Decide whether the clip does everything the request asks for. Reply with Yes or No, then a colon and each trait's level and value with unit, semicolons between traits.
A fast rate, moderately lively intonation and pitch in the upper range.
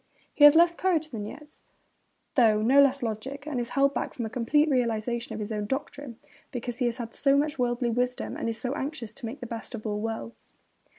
Yes: fast, 220 wpm; average, 3.7 semitones; high, 245 Hz